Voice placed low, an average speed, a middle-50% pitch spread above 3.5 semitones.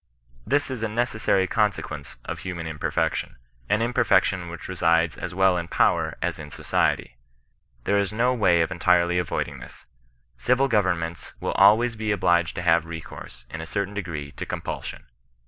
Yes: very low, 90 Hz; average, 170 wpm; average, 4.3 semitones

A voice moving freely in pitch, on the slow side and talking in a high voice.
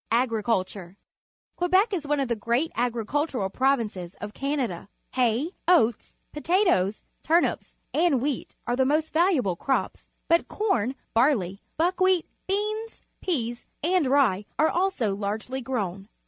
Yes: wide, 7.3 semitones; slow, 130 wpm; very high, 260 Hz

